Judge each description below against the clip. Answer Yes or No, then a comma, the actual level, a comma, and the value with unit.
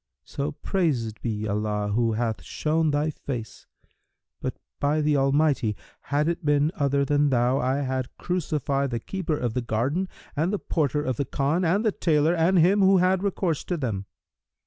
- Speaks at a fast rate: No, average, 175 wpm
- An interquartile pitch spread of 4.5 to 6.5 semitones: Yes, average, 4.8 semitones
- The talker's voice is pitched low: No, medium, 145 Hz